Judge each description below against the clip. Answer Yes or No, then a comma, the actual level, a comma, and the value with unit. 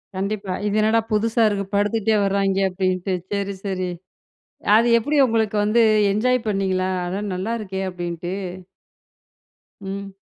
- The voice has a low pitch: No, high, 200 Hz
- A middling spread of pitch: No, narrow, 2.3 semitones